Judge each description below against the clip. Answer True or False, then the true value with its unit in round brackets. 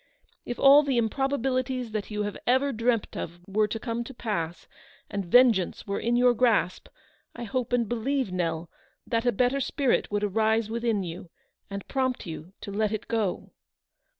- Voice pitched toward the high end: True (225 Hz)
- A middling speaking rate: True (175 wpm)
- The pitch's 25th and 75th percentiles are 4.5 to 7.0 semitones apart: False (3.7 semitones)